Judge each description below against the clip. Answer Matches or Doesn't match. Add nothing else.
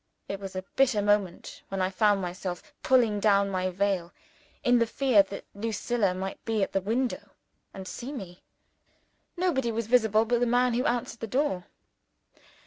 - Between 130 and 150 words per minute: Doesn't match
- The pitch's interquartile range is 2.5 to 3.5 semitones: Doesn't match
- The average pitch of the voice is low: Doesn't match